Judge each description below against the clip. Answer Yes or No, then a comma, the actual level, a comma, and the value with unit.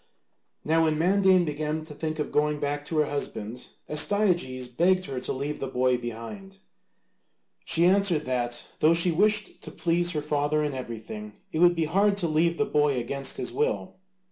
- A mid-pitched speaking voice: Yes, medium, 155 Hz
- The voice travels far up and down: No, average, 4.3 semitones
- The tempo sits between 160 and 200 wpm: Yes, average, 180 wpm